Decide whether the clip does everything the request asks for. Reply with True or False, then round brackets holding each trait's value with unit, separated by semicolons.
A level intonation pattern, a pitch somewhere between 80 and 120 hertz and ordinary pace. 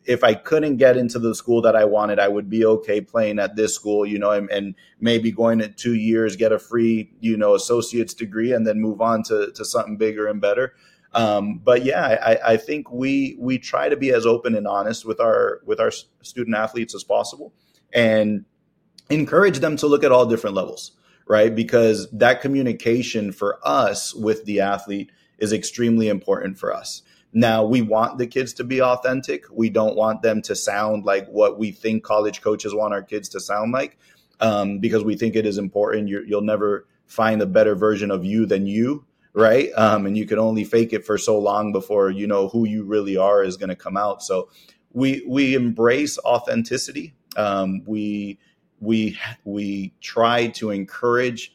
True (2.2 semitones; 110 Hz; 195 wpm)